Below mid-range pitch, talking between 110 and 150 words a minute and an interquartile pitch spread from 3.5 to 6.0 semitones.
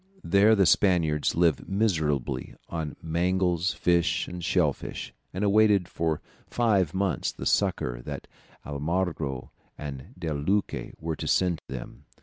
Yes: very low, 85 Hz; slow, 135 wpm; average, 4.0 semitones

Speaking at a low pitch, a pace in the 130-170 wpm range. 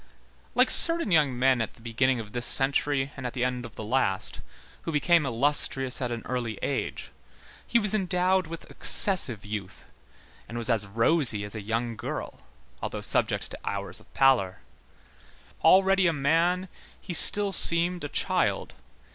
Yes: low, 130 Hz; average, 160 wpm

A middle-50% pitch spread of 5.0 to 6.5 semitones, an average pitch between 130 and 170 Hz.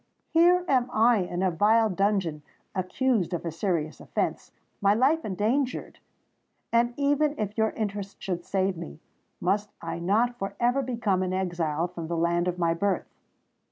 No: average, 5.3 semitones; high, 200 Hz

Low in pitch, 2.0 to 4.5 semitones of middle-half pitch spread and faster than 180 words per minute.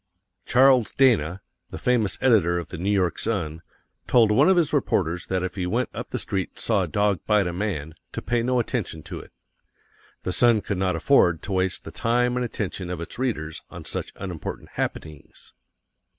No: low, 100 Hz; average, 5.2 semitones; average, 195 wpm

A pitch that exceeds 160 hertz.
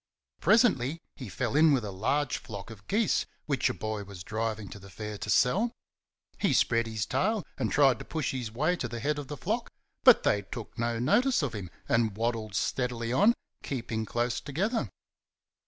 No: low, 120 Hz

